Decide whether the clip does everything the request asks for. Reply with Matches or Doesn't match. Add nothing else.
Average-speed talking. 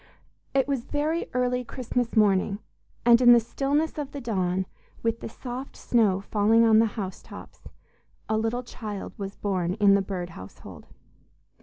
Matches